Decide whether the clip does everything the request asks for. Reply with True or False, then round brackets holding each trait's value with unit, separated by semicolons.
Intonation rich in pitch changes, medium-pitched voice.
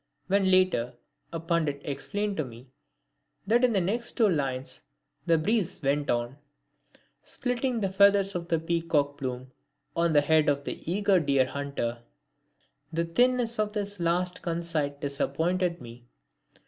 True (5.8 semitones; 170 Hz)